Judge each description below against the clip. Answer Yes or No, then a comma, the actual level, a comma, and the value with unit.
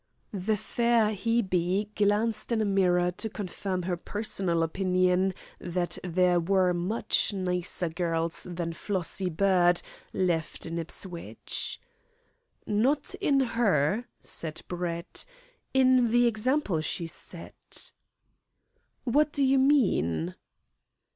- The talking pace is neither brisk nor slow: No, slow, 110 wpm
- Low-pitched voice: No, medium, 185 Hz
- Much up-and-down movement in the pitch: No, average, 4.1 semitones